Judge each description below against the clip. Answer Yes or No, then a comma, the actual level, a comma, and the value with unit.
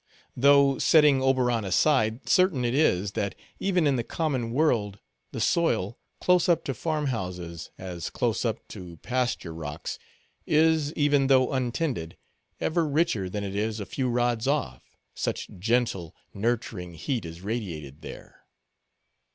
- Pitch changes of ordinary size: No, wide, 6.8 semitones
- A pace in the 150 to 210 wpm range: No, average, 140 wpm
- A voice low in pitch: Yes, low, 120 Hz